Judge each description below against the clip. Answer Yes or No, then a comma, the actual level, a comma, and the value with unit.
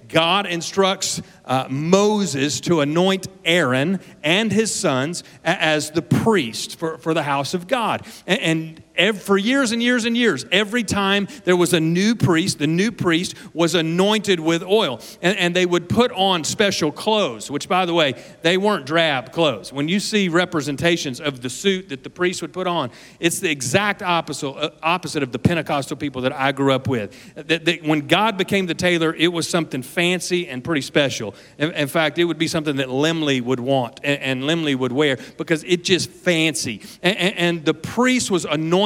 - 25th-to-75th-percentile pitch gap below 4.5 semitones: Yes, average, 3.9 semitones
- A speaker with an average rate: Yes, average, 195 wpm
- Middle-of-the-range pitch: Yes, medium, 170 Hz